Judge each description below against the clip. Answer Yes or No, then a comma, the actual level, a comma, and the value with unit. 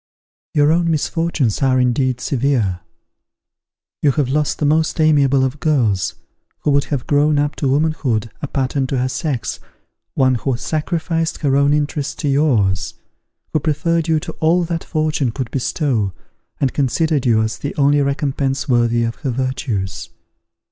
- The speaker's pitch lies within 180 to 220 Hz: No, medium, 140 Hz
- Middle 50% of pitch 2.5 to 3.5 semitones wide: Yes, average, 3.1 semitones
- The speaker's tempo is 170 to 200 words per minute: No, average, 155 wpm